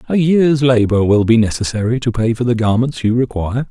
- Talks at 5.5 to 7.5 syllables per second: Yes, 5.7 syllables/s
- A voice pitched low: Yes, low, 120 Hz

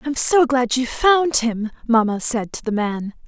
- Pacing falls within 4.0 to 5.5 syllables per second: Yes, 4.1 syllables/s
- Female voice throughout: Yes, female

